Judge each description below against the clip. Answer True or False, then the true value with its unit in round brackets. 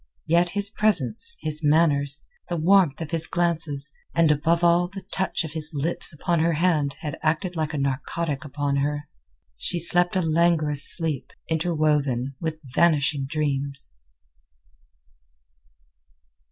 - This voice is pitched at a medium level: True (155 Hz)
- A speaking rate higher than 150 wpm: False (135 wpm)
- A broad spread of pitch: False (2.9 semitones)